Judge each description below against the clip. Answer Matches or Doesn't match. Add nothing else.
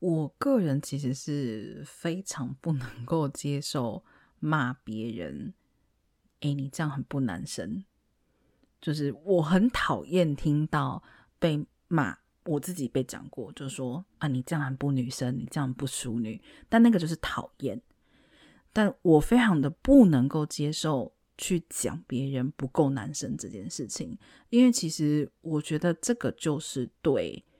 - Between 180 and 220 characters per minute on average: Matches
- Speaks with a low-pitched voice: Doesn't match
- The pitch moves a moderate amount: Matches